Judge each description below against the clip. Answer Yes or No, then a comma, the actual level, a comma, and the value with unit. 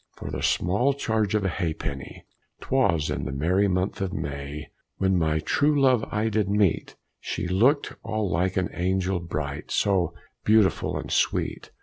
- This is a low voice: Yes, very low, 95 Hz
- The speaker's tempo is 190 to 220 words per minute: No, average, 160 wpm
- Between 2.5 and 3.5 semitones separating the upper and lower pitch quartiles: No, average, 4.1 semitones